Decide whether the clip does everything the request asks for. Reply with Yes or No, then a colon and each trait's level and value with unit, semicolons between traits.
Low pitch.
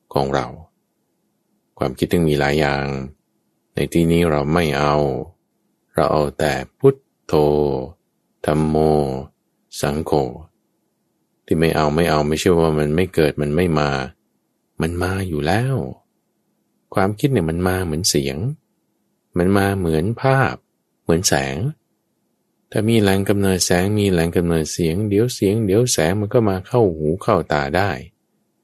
Yes: very low, 85 Hz